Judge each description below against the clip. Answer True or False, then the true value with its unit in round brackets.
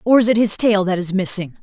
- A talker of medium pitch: False (200 Hz)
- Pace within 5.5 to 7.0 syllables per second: True (6.0 syllables/s)